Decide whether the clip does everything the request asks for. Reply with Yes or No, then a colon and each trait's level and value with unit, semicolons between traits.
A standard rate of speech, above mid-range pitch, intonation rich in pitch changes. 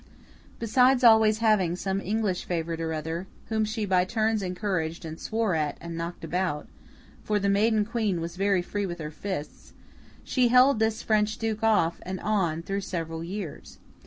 No: average, 160 wpm; high, 195 Hz; average, 4.4 semitones